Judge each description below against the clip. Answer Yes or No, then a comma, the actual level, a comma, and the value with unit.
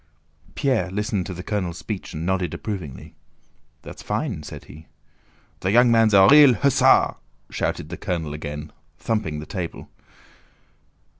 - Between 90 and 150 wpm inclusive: Yes, average, 140 wpm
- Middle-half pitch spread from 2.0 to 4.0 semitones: No, wide, 5.5 semitones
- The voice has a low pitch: Yes, very low, 95 Hz